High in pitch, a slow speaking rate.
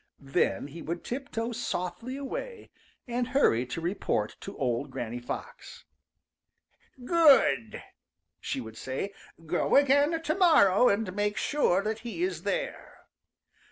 Yes: high, 215 Hz; slow, 125 wpm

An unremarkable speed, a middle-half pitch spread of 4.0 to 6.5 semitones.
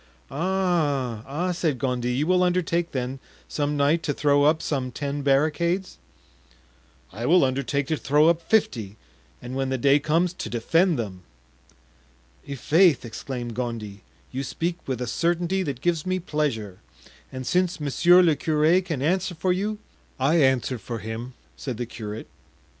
Yes: average, 155 wpm; average, 5.2 semitones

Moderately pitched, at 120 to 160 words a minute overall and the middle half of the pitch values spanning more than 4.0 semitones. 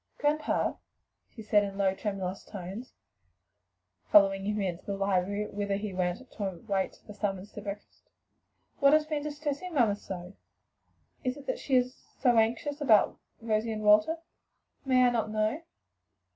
No: high, 210 Hz; average, 155 wpm; average, 4.4 semitones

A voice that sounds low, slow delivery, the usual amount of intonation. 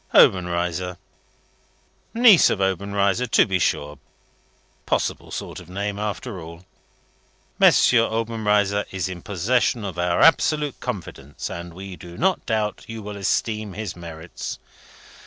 Yes: low, 100 Hz; slow, 125 wpm; average, 3.8 semitones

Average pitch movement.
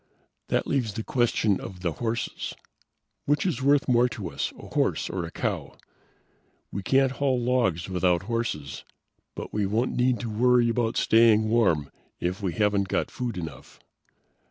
Yes: average, 4.6 semitones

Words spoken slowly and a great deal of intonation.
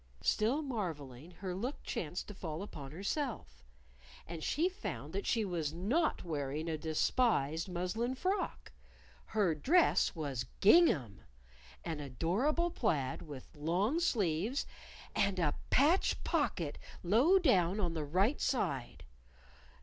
Yes: slow, 125 wpm; wide, 8.3 semitones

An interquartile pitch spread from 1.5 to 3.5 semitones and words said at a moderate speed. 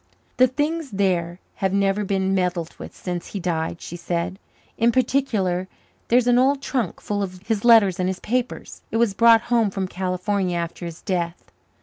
No: average, 4.4 semitones; average, 180 wpm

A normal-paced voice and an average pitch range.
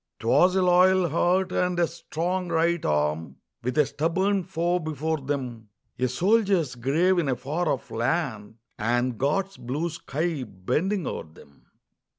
No: average, 150 wpm; wide, 6.0 semitones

